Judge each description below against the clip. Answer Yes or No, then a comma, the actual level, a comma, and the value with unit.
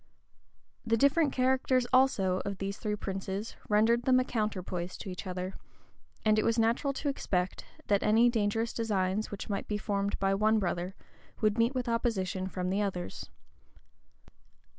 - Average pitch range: Yes, average, 3.4 semitones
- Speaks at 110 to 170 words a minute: Yes, average, 160 wpm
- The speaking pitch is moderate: No, high, 210 Hz